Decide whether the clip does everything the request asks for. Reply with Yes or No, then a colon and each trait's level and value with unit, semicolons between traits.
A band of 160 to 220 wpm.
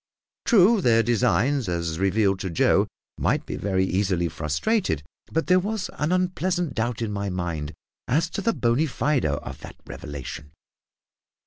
No: average, 150 wpm